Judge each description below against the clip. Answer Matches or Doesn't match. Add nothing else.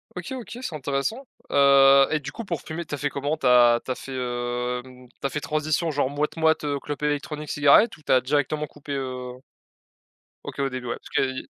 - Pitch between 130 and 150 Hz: Matches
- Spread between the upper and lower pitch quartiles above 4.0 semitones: Doesn't match